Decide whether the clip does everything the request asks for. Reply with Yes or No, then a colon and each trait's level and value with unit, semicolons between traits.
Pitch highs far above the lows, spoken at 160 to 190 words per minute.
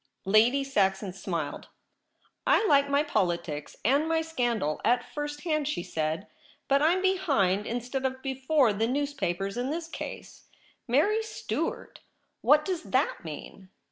No: wide, 7.3 semitones; average, 150 wpm